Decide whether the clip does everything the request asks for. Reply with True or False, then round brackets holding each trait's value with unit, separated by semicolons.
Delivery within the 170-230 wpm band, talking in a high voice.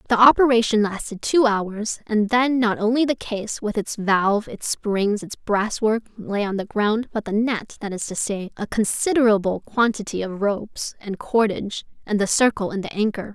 True (190 wpm; 215 Hz)